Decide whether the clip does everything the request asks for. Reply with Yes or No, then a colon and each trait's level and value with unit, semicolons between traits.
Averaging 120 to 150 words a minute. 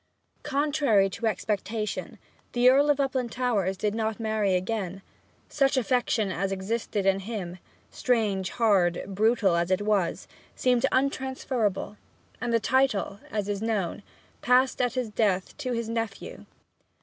Yes: slow, 135 wpm